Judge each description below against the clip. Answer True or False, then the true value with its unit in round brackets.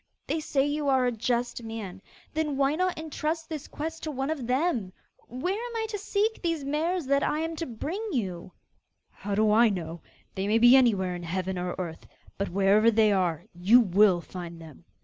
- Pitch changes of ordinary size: False (8.3 semitones)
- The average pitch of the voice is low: False (240 Hz)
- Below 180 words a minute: False (205 wpm)